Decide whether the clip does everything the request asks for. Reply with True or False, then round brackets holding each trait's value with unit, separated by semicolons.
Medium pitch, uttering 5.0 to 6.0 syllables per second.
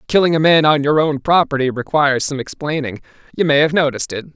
False (145 Hz; 6.4 syllables/s)